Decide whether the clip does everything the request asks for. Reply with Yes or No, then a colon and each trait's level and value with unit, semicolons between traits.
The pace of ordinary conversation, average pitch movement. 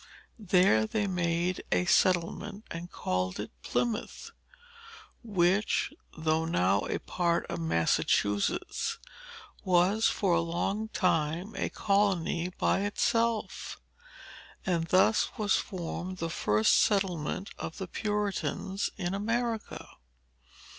No: slow, 105 wpm; average, 3.6 semitones